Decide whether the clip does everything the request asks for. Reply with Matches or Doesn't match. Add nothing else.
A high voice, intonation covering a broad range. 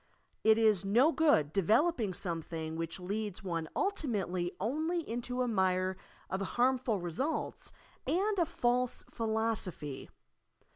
Matches